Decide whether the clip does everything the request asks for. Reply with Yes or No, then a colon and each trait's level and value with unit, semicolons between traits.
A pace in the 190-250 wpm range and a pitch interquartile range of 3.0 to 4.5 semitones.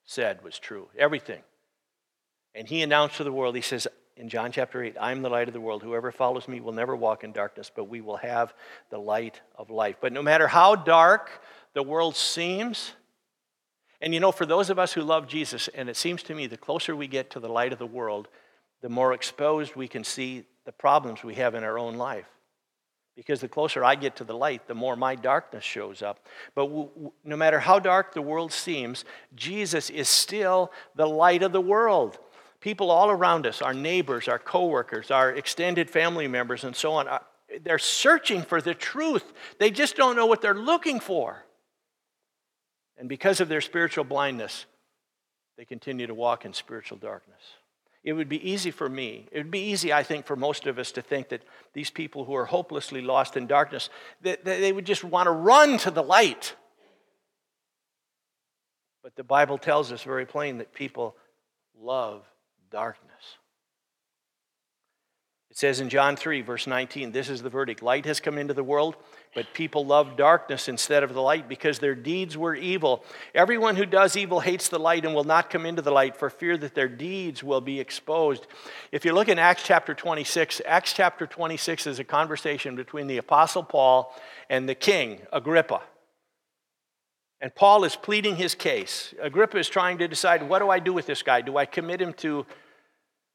No: average, 195 wpm; average, 5.2 semitones